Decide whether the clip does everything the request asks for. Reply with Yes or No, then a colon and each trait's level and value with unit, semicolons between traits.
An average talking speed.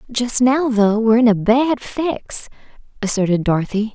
Yes: average, 150 wpm